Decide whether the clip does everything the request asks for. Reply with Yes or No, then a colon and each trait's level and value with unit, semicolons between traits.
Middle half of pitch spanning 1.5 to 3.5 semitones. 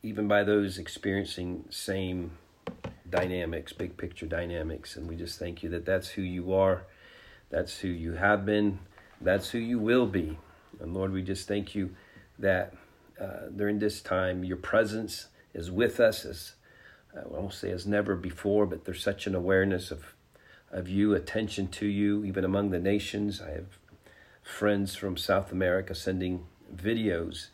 Yes: narrow, 2.4 semitones